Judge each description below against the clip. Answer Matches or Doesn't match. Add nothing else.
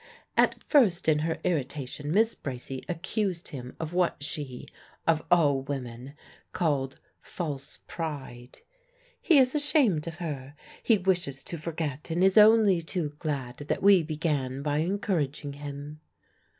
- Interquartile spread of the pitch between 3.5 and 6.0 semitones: Matches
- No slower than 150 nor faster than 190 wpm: Doesn't match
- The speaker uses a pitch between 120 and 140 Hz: Doesn't match